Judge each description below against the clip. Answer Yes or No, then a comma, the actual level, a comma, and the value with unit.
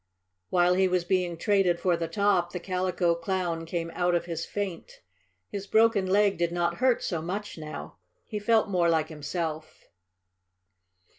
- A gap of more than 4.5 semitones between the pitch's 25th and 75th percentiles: No, narrow, 2.6 semitones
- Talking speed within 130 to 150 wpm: No, average, 160 wpm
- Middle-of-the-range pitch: Yes, medium, 180 Hz